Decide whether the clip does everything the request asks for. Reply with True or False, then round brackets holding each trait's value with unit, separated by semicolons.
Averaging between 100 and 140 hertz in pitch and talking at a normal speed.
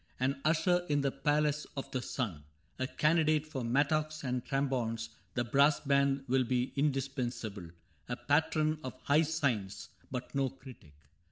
True (135 Hz; 150 wpm)